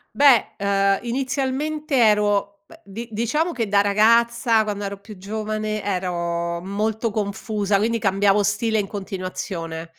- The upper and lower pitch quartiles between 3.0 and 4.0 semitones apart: No, narrow, 2.6 semitones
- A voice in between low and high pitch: No, high, 210 Hz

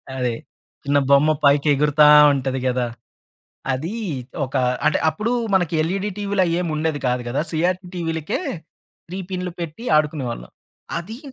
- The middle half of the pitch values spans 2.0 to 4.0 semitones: No, average, 4.5 semitones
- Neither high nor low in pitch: Yes, medium, 155 Hz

